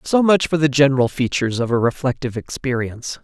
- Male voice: Yes, male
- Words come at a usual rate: Yes, average, 185 wpm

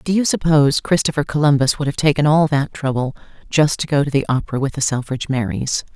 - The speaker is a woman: Yes, female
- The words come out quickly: Yes, fast, 210 wpm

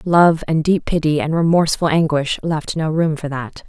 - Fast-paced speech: No, average, 195 wpm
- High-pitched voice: No, medium, 160 Hz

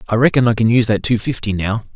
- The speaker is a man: Yes, male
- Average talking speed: No, fast, 275 wpm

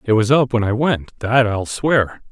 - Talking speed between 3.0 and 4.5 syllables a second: Yes, 4.4 syllables/s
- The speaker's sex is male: Yes, male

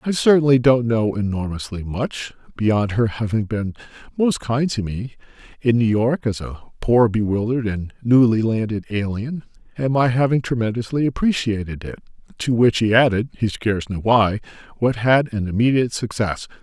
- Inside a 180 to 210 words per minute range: No, average, 155 wpm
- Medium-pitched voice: No, low, 115 Hz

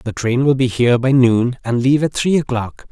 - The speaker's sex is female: No, male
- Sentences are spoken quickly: Yes, fast, 245 wpm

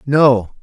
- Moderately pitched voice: No, low, 130 Hz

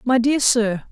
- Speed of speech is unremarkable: Yes, average, 195 wpm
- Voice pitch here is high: Yes, high, 240 Hz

